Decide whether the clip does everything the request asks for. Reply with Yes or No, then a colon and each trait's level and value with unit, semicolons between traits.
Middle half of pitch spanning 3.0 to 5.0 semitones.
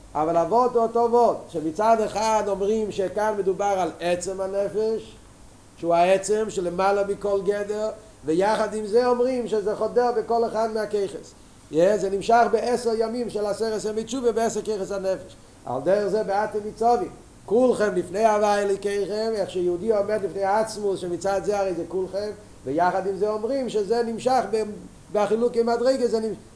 No: narrow, 2.6 semitones